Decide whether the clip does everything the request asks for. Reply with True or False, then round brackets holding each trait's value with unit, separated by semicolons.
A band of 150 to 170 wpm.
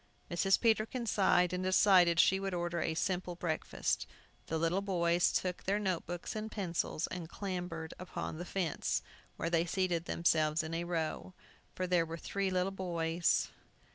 True (165 wpm)